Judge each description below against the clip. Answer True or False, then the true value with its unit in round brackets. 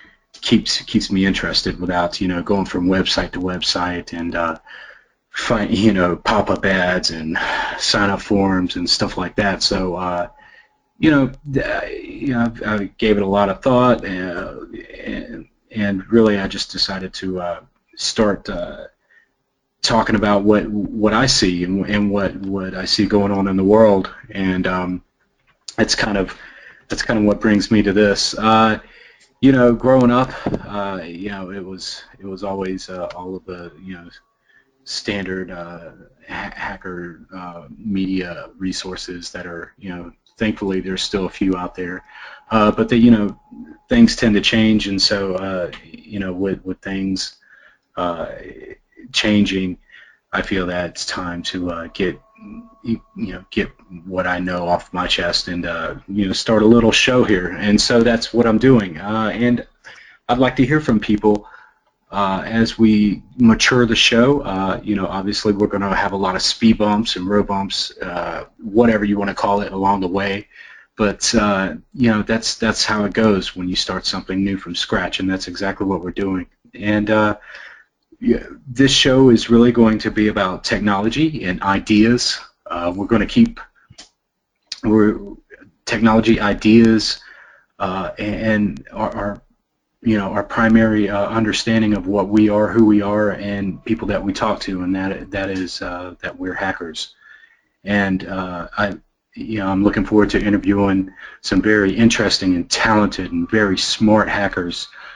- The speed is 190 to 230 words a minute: False (175 wpm)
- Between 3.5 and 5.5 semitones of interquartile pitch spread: False (2.9 semitones)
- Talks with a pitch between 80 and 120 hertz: True (100 Hz)